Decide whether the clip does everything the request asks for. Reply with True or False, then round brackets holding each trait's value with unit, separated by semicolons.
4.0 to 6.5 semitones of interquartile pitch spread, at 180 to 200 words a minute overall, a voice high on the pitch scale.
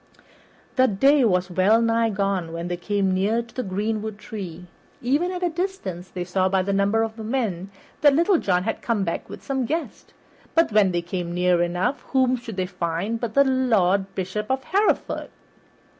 True (5.4 semitones; 190 wpm; 210 Hz)